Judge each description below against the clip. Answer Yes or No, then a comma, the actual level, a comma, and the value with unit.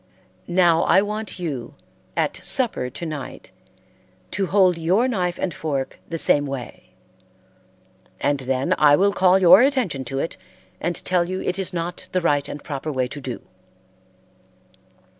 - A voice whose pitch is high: No, medium, 170 Hz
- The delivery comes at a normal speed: Yes, average, 155 wpm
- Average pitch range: Yes, average, 4.7 semitones